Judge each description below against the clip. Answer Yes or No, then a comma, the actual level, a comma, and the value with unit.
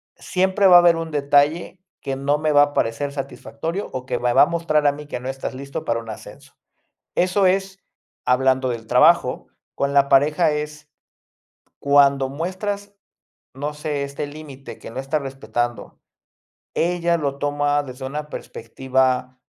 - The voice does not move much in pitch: No, average, 3.1 semitones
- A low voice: No, medium, 145 Hz